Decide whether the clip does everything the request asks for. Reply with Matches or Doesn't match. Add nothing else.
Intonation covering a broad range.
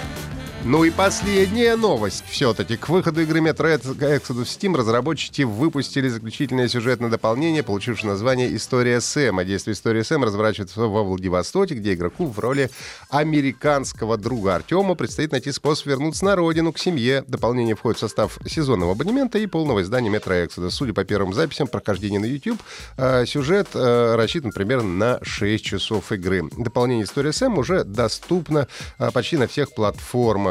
Matches